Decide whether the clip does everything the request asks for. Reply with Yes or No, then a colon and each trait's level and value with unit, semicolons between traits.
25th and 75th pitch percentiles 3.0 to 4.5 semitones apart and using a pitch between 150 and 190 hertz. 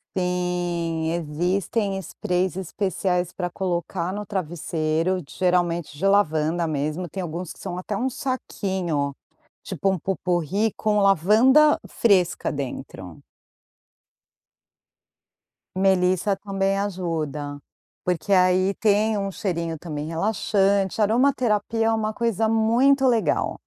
Yes: average, 3.5 semitones; medium, 185 Hz